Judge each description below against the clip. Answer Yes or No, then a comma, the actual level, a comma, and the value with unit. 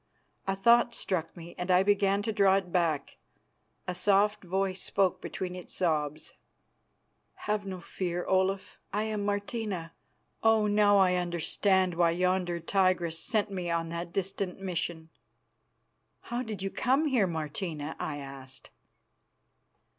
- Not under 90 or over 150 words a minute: Yes, average, 140 wpm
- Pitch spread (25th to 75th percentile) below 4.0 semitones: Yes, average, 2.9 semitones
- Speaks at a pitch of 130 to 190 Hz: Yes, medium, 185 Hz